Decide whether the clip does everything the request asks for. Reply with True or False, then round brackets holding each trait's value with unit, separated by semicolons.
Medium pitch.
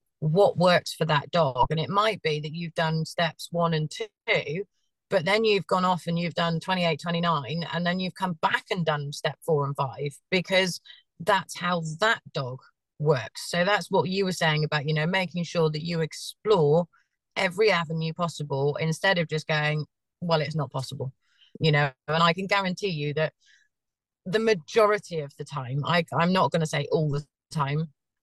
True (165 Hz)